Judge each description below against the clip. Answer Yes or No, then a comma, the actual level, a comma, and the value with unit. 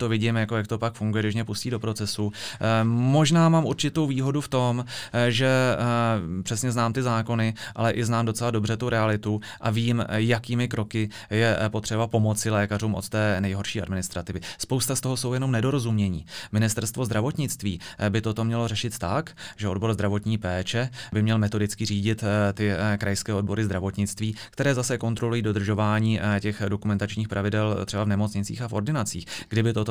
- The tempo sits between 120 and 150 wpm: No, average, 165 wpm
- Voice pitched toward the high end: No, low, 110 Hz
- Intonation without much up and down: Yes, narrow, 2.2 semitones